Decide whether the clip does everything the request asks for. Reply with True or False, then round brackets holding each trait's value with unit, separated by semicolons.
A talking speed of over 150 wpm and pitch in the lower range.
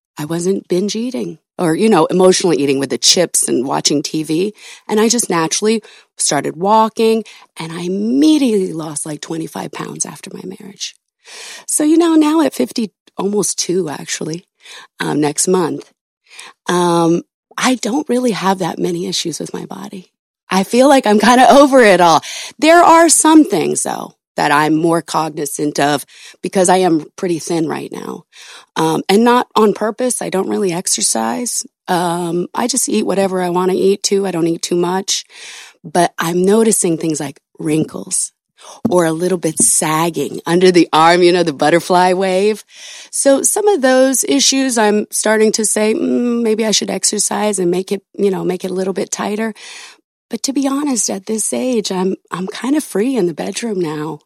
False (180 wpm; 190 Hz)